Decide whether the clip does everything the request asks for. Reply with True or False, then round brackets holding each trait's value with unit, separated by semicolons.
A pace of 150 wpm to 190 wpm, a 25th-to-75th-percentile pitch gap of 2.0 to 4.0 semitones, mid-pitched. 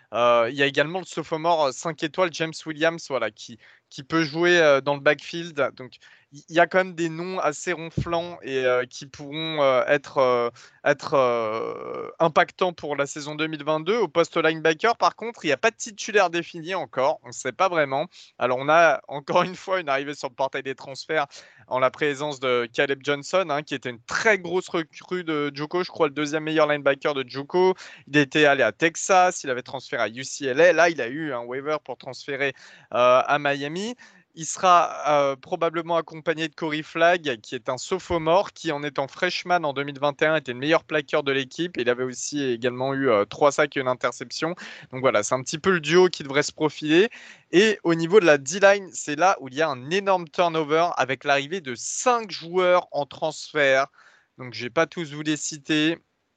False (205 wpm; 3.7 semitones; 155 Hz)